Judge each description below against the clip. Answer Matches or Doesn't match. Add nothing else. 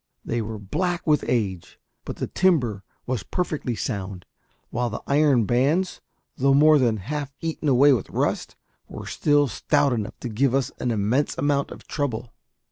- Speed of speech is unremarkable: Matches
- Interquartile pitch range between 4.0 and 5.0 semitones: Matches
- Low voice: Matches